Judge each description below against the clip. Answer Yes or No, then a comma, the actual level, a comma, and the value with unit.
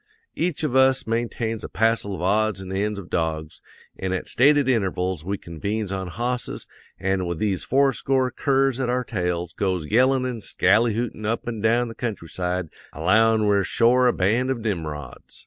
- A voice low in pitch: Yes, low, 110 Hz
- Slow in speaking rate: No, average, 175 wpm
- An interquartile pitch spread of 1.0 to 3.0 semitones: No, average, 4.8 semitones